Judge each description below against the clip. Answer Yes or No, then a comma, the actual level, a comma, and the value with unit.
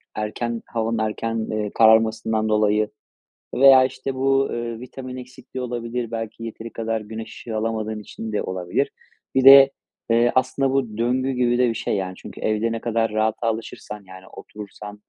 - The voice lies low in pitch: Yes, low, 115 Hz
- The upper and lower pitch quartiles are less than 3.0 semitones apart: Yes, narrow, 2.4 semitones